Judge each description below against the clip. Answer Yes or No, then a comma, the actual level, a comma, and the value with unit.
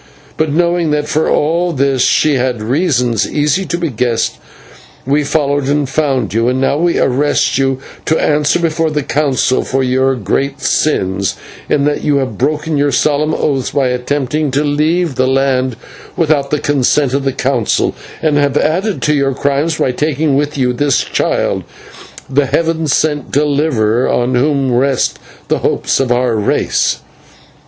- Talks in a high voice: No, medium, 140 Hz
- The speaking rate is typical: Yes, average, 165 wpm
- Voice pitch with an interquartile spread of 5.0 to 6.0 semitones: No, average, 2.7 semitones